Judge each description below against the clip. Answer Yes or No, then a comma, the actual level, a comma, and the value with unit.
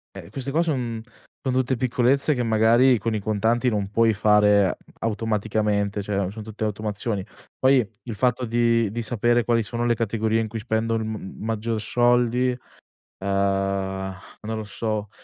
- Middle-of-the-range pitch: No, low, 115 Hz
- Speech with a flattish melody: Yes, narrow, 2.2 semitones